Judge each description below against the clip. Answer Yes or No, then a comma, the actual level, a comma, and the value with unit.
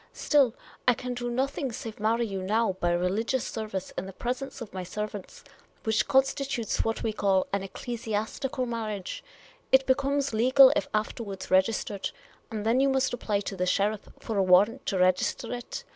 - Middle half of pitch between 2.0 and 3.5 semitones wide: No, average, 4.1 semitones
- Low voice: No, high, 220 Hz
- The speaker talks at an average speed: Yes, average, 180 wpm